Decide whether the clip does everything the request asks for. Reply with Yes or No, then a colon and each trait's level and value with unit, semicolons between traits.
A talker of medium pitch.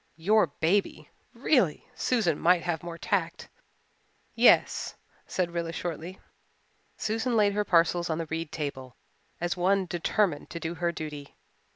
Yes: medium, 170 Hz